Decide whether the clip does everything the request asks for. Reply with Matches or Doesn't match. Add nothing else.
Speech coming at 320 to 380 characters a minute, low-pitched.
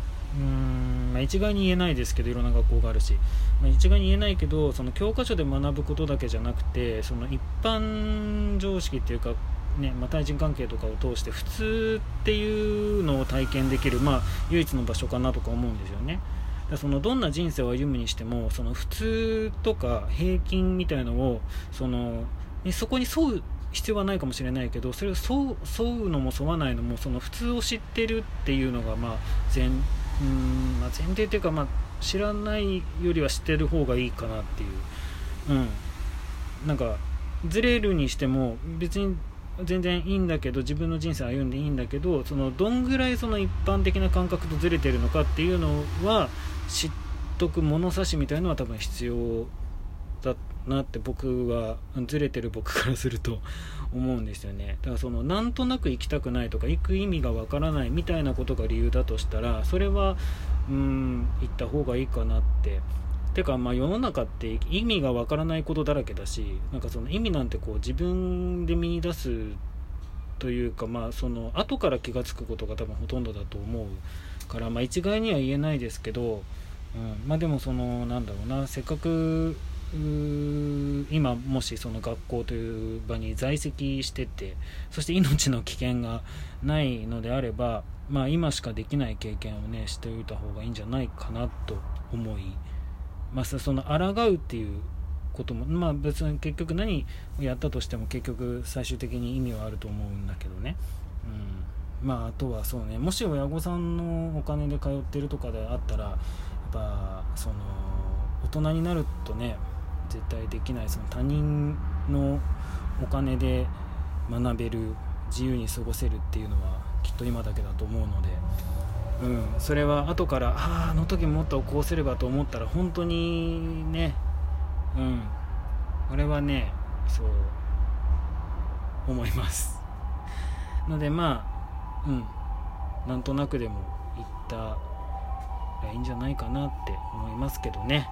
Matches